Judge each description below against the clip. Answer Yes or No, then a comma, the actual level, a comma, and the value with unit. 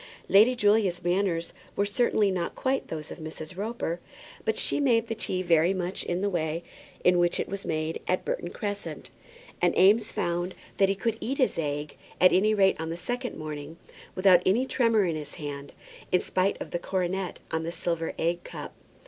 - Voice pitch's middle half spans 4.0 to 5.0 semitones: No, average, 3.6 semitones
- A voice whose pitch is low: No, medium, 185 Hz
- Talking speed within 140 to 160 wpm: No, average, 190 wpm